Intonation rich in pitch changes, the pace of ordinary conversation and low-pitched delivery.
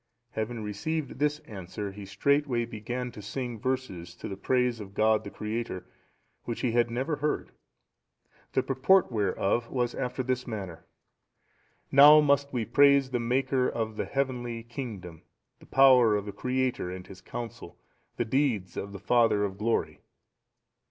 No: average, 4.0 semitones; average, 155 wpm; low, 120 Hz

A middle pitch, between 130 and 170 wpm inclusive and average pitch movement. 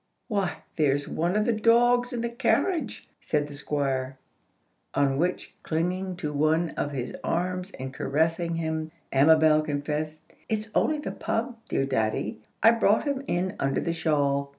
No: medium, 160 Hz; average, 155 wpm; wide, 6.7 semitones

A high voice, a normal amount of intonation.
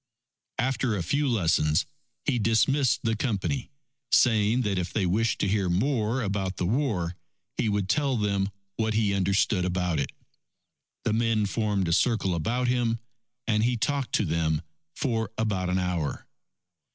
No: low, 105 Hz; average, 4.2 semitones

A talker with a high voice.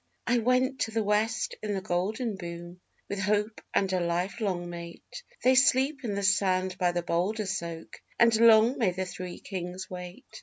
Yes: high, 195 Hz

